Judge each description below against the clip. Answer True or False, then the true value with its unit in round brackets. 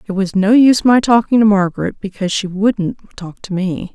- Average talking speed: False (215 wpm)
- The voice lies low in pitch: False (200 Hz)